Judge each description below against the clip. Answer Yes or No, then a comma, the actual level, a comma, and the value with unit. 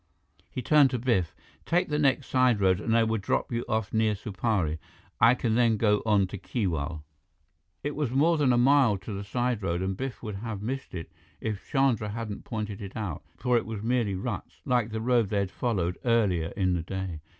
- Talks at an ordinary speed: No, fast, 210 wpm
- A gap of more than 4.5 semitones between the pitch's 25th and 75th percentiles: No, average, 4.1 semitones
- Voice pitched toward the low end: Yes, low, 110 Hz